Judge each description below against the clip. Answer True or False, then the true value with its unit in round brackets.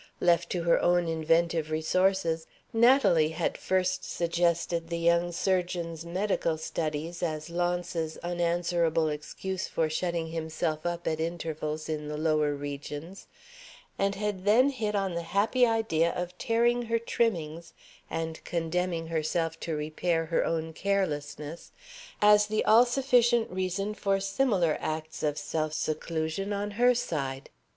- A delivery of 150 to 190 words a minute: False (135 wpm)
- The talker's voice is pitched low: False (170 Hz)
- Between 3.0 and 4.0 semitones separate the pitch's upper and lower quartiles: True (3.5 semitones)